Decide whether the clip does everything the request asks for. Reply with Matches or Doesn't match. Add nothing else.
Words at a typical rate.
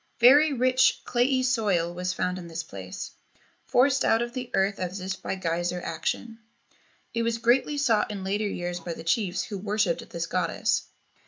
Matches